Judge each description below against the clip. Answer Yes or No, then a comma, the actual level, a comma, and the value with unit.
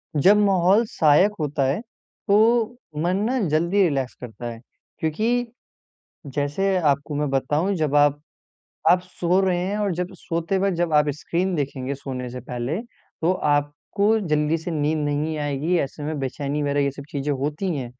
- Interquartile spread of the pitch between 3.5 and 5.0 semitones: Yes, average, 4.1 semitones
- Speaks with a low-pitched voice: No, medium, 150 Hz